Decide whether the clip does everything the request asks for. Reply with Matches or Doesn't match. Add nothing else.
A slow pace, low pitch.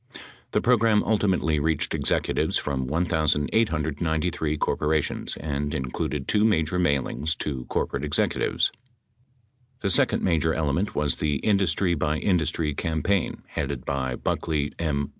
Matches